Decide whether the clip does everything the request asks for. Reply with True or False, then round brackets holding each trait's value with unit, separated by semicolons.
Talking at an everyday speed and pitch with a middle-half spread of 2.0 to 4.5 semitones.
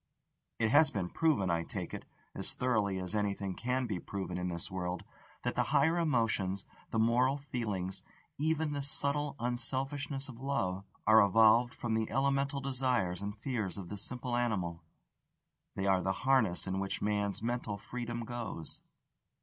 False (160 wpm; 5.2 semitones)